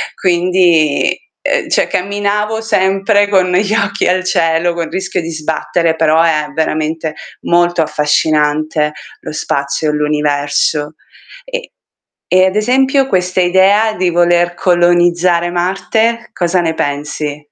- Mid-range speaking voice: Yes, medium, 175 Hz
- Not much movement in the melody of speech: No, average, 3.4 semitones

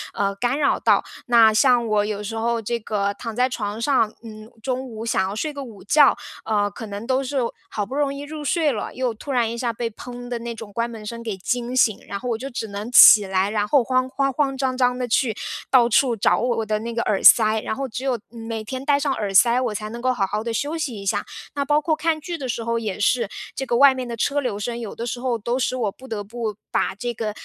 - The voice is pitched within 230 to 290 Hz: Yes, high, 235 Hz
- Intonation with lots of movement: No, average, 3.2 semitones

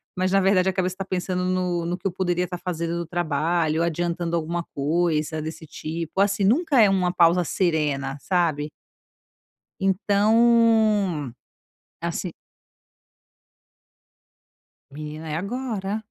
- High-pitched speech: No, medium, 175 Hz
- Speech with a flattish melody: No, average, 3.0 semitones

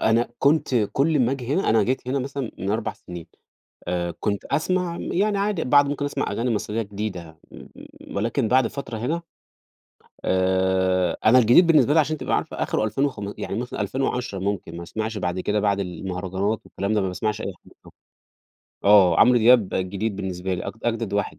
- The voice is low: Yes, low, 110 Hz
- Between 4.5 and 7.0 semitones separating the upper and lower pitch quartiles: Yes, wide, 5.5 semitones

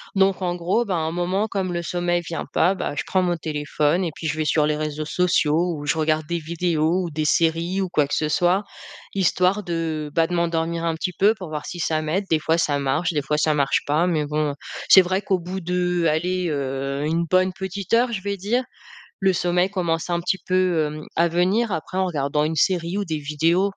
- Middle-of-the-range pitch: Yes, medium, 170 Hz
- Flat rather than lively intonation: No, average, 3.0 semitones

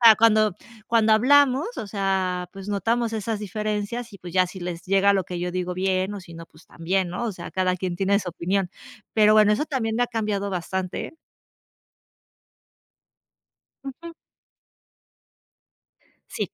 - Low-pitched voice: No, high, 200 Hz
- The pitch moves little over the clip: No, average, 3.3 semitones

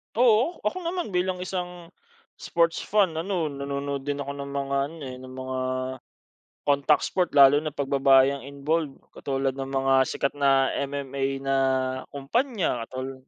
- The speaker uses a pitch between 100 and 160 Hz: Yes, medium, 140 Hz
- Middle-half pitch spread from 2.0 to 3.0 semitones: No, average, 4.0 semitones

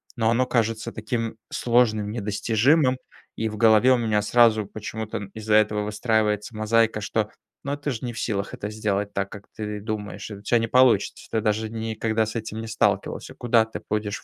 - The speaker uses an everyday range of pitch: No, narrow, 1.5 semitones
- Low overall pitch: Yes, low, 110 Hz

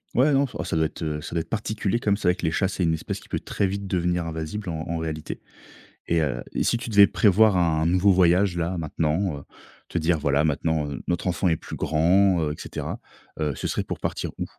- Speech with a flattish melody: No, average, 3.6 semitones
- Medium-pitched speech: No, very low, 85 Hz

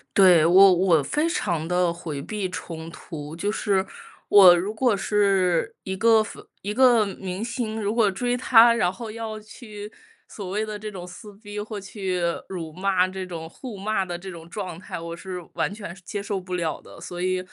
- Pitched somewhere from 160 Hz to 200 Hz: Yes, high, 195 Hz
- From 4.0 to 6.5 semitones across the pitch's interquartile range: No, average, 3.2 semitones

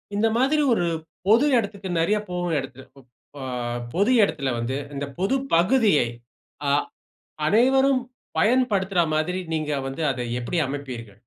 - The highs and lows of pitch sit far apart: Yes, wide, 8.0 semitones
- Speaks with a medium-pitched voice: Yes, medium, 180 Hz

